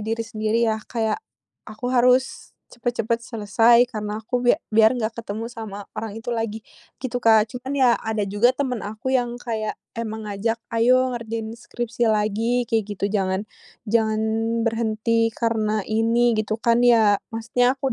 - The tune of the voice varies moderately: No, narrow, 1.8 semitones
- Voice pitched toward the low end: No, high, 225 Hz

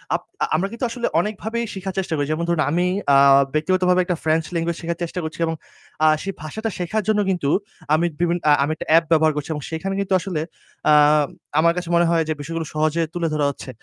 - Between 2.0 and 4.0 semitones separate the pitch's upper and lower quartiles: Yes, average, 2.9 semitones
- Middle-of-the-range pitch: Yes, medium, 170 Hz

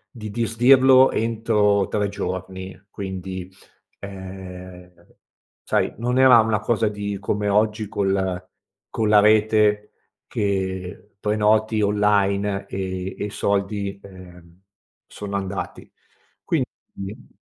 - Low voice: Yes, low, 100 Hz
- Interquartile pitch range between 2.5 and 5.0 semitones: No, narrow, 2.1 semitones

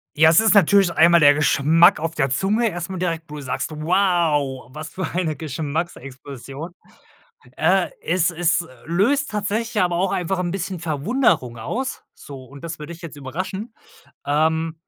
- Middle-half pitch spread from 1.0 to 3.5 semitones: No, average, 3.9 semitones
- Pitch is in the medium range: Yes, medium, 165 Hz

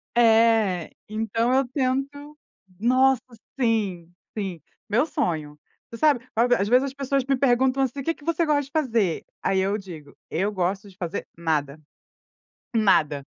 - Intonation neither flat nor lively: No, wide, 5.9 semitones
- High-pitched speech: Yes, high, 230 Hz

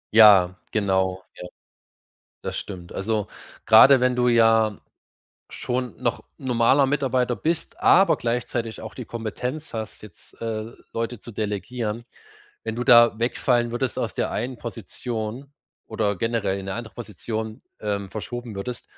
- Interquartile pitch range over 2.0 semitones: Yes, narrow, 2.6 semitones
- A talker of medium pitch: No, low, 115 Hz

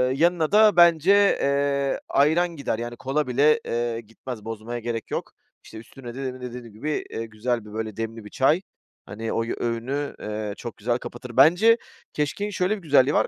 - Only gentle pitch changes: No, average, 4.9 semitones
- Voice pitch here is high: No, low, 125 Hz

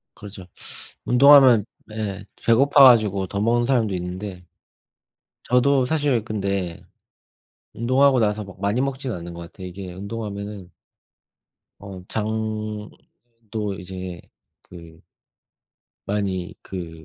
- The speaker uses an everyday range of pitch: Yes, average, 4.0 semitones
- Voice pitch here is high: No, low, 105 Hz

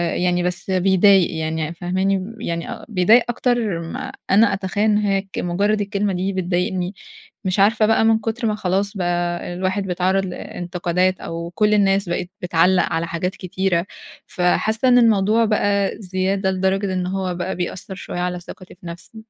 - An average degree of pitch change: No, narrow, 2.3 semitones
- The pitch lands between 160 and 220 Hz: Yes, high, 190 Hz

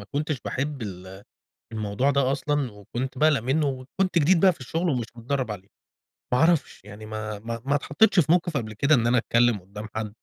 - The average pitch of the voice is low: Yes, low, 130 Hz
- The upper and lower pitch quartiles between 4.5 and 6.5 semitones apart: Yes, average, 5.2 semitones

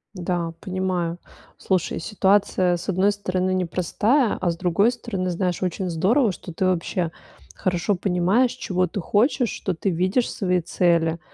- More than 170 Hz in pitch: Yes, medium, 185 Hz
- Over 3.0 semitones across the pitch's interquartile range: No, narrow, 2.5 semitones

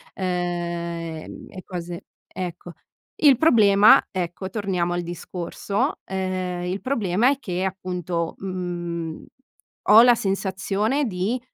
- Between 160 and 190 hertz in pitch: Yes, medium, 185 Hz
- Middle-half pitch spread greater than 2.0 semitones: Yes, narrow, 2.4 semitones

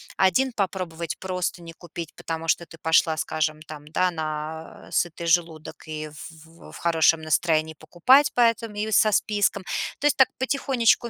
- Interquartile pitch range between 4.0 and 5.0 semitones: Yes, average, 4.5 semitones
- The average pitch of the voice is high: No, medium, 170 Hz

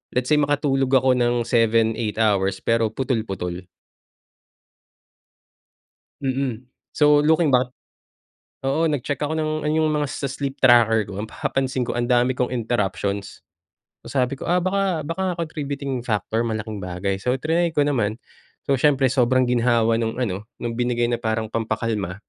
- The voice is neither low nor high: No, low, 125 Hz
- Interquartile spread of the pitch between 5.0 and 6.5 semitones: No, average, 4.1 semitones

